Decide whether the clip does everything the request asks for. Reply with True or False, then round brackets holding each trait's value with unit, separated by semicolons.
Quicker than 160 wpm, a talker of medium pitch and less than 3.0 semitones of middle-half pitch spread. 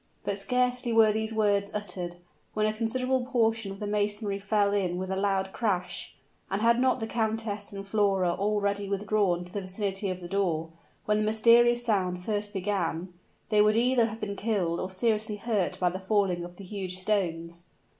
False (185 wpm; 205 Hz; 2.6 semitones)